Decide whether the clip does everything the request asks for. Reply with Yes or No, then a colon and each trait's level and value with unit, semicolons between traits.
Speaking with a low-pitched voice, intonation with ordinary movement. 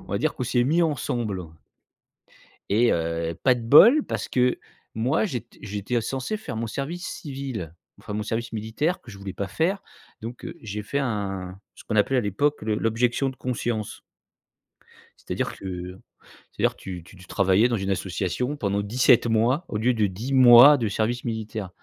Yes: low, 115 Hz; average, 4.3 semitones